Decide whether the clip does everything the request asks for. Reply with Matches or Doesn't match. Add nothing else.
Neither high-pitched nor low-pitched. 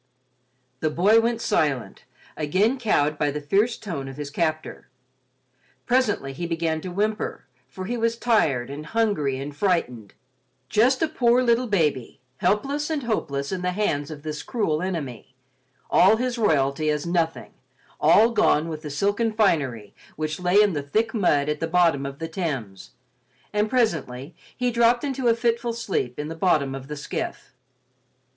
Matches